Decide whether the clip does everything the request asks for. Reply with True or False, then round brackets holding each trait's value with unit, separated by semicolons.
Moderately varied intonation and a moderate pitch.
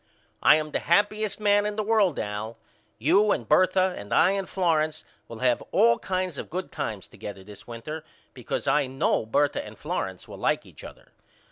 False (8.4 semitones; 155 Hz)